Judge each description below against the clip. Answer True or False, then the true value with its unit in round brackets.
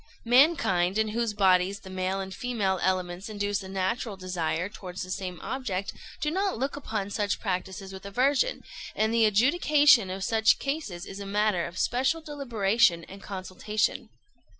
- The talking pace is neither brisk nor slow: True (160 wpm)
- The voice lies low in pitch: False (200 Hz)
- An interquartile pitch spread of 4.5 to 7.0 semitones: False (4.1 semitones)